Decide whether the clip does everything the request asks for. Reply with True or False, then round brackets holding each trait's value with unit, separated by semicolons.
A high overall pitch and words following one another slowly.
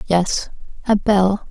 True (195 Hz; 120 wpm)